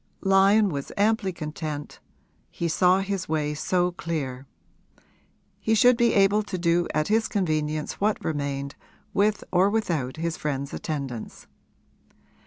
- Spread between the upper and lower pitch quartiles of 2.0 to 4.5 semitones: No, average, 5.0 semitones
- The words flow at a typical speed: No, slow, 130 wpm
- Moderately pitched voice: Yes, medium, 170 Hz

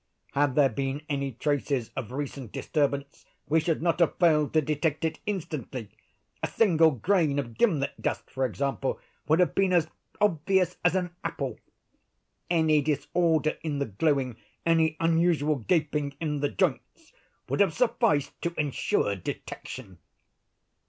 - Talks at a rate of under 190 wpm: Yes, average, 140 wpm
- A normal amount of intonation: Yes, average, 3.3 semitones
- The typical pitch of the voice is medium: Yes, medium, 150 Hz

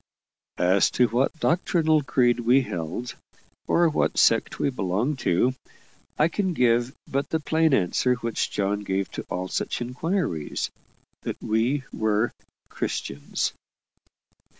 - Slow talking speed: Yes, slow, 125 wpm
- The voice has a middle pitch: No, low, 125 Hz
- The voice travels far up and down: Yes, wide, 6.3 semitones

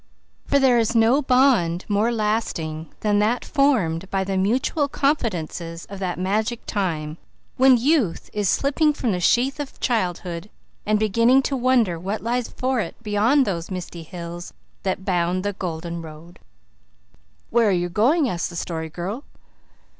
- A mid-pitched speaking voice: No, high, 205 Hz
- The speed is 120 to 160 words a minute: Yes, average, 155 wpm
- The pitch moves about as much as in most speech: No, wide, 6.0 semitones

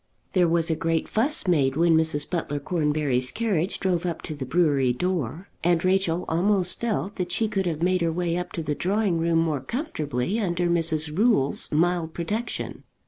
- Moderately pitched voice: Yes, medium, 170 Hz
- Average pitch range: Yes, average, 3.1 semitones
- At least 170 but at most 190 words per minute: Yes, average, 185 wpm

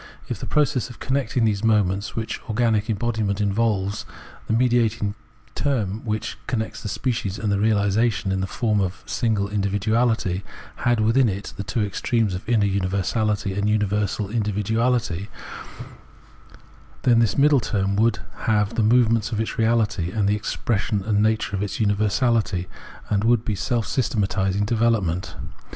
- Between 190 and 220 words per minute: No, average, 155 wpm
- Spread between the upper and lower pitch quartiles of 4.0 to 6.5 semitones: No, narrow, 2.4 semitones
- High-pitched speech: No, low, 110 Hz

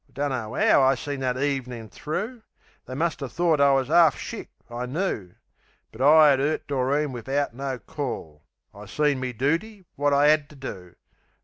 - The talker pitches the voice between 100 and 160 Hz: Yes, medium, 140 Hz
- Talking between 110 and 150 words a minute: No, average, 180 wpm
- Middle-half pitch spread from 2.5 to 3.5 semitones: Yes, average, 3.1 semitones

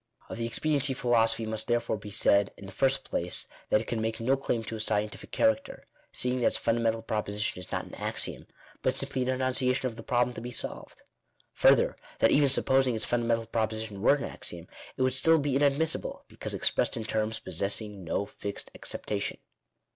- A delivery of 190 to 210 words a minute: Yes, average, 200 wpm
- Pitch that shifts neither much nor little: Yes, average, 3.1 semitones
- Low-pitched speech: Yes, low, 115 Hz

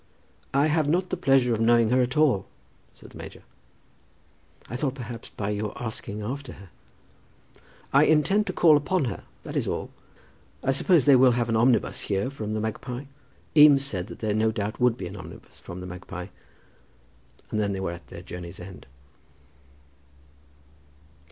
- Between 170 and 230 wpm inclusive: Yes, average, 175 wpm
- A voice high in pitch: No, low, 120 Hz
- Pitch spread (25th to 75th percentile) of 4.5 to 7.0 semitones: Yes, average, 5.2 semitones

